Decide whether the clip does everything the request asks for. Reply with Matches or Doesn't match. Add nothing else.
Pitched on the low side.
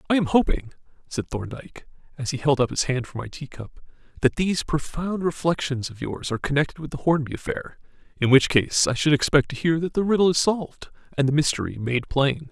Doesn't match